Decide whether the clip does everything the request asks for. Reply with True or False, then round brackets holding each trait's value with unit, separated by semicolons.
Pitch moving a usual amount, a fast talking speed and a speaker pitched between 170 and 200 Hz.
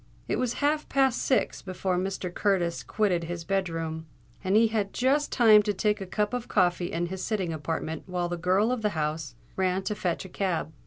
True (3.7 semitones; 210 wpm; 190 Hz)